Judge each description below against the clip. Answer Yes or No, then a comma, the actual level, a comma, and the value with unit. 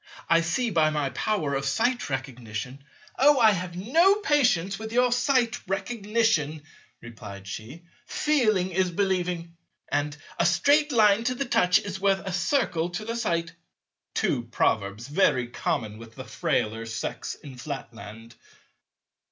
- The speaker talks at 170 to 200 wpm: No, average, 140 wpm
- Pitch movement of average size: No, wide, 8.8 semitones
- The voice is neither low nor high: Yes, medium, 175 Hz